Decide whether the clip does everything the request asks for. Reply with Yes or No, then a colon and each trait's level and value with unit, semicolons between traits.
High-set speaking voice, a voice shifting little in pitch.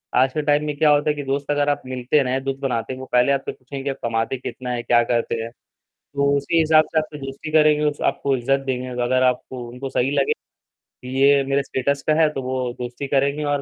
No: low, 135 Hz; narrow, 2.3 semitones